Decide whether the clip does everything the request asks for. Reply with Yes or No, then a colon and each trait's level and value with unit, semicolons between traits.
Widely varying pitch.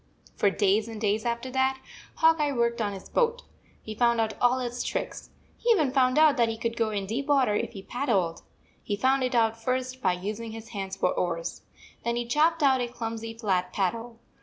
No: average, 3.5 semitones